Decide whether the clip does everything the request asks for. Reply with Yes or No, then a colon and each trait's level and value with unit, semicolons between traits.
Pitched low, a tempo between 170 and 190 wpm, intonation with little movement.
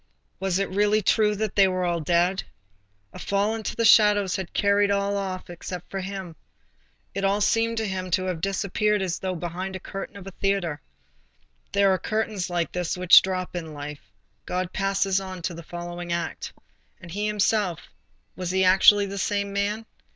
No: high, 190 Hz; average, 175 wpm; narrow, 2.1 semitones